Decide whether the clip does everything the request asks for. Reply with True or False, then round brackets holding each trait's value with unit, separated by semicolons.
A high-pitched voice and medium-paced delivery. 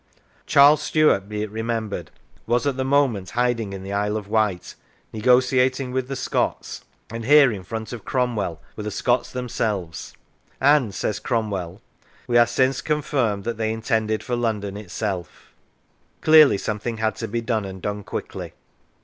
False (115 Hz; 165 wpm)